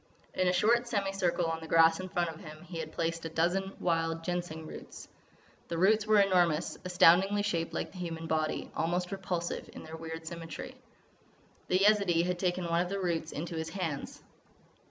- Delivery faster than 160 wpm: Yes, average, 190 wpm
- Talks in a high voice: No, medium, 175 Hz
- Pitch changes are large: No, narrow, 2.4 semitones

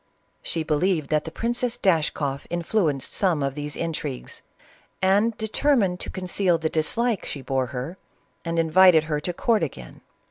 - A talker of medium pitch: Yes, medium, 165 Hz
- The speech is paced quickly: No, average, 150 wpm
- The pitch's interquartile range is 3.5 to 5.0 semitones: Yes, average, 4.5 semitones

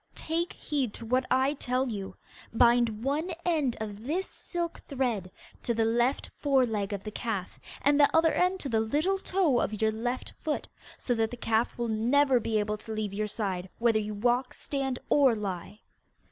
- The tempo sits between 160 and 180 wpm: No, average, 190 wpm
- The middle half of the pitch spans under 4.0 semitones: No, average, 4.4 semitones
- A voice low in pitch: No, high, 240 Hz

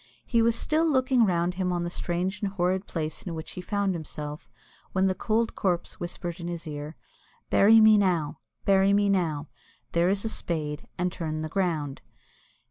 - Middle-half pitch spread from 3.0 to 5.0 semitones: Yes, average, 3.6 semitones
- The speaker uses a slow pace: No, average, 185 wpm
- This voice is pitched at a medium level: Yes, medium, 180 Hz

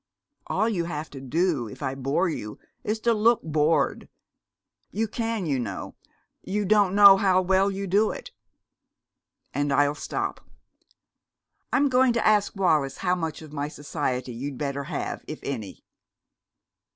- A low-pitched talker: No, medium, 165 Hz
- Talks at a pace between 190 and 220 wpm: No, average, 150 wpm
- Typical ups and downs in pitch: No, wide, 6.3 semitones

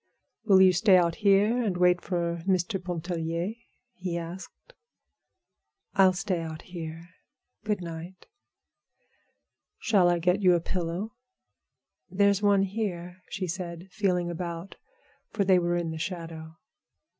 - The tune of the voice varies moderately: No, narrow, 2.3 semitones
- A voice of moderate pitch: Yes, medium, 180 Hz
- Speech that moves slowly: Yes, slow, 130 wpm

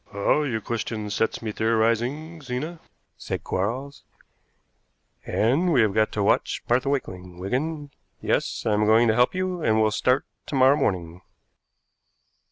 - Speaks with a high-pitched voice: No, low, 115 Hz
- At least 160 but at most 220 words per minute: No, average, 150 wpm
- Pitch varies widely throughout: No, average, 4.8 semitones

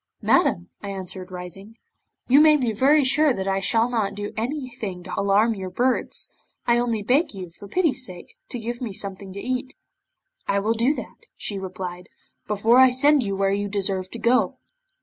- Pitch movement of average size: Yes, average, 4.5 semitones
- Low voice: No, high, 215 Hz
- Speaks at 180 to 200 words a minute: Yes, average, 190 wpm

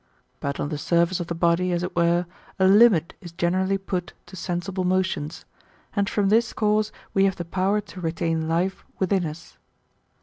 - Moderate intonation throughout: No, narrow, 2.3 semitones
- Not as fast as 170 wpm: No, average, 180 wpm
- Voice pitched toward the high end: No, medium, 180 Hz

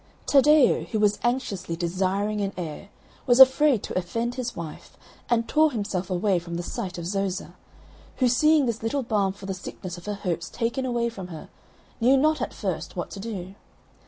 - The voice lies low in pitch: No, high, 210 Hz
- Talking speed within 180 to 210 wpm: Yes, average, 190 wpm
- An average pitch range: Yes, average, 5.0 semitones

